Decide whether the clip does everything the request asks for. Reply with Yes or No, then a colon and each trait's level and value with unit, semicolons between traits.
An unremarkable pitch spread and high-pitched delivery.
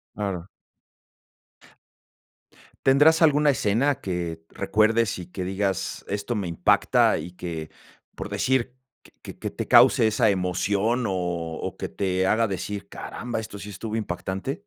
No: average, 4.2 semitones; low, 100 Hz